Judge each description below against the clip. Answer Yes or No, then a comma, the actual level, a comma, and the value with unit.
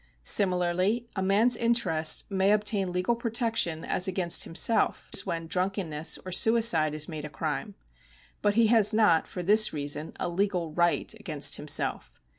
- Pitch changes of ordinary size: Yes, average, 4.7 semitones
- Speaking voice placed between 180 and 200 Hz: Yes, medium, 185 Hz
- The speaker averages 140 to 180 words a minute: Yes, average, 155 wpm